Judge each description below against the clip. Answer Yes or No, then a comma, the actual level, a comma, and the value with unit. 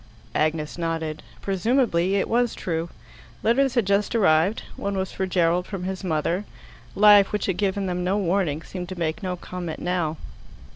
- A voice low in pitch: No, medium, 185 Hz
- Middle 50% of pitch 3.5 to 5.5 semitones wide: No, average, 3.1 semitones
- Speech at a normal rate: Yes, average, 165 wpm